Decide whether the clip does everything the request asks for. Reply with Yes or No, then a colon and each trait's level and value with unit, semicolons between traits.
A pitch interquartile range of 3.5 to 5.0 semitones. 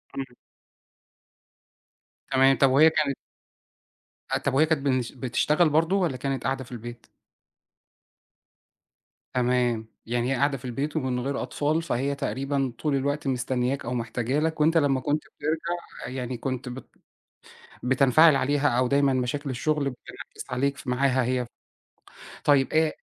No: narrow, 2.6 semitones